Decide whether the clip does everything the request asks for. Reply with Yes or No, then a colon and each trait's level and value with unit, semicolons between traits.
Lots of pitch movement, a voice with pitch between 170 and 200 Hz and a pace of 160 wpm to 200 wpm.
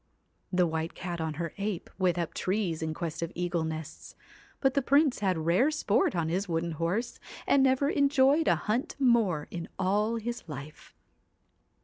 Yes: wide, 6.4 semitones; medium, 185 Hz; average, 170 wpm